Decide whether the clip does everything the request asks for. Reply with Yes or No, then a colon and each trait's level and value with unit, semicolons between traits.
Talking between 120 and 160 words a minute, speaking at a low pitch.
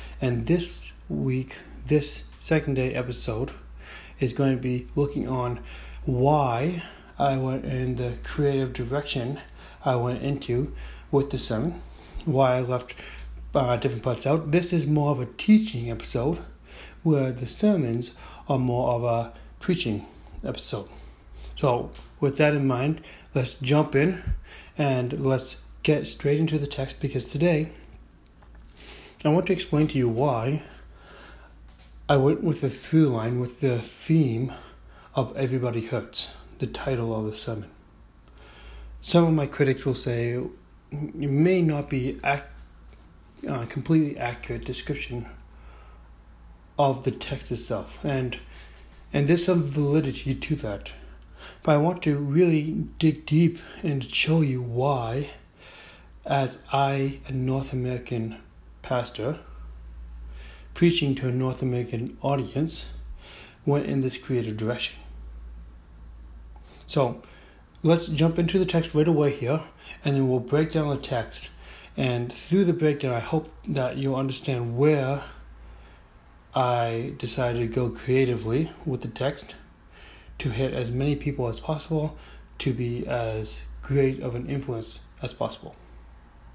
Yes: slow, 135 wpm; low, 130 Hz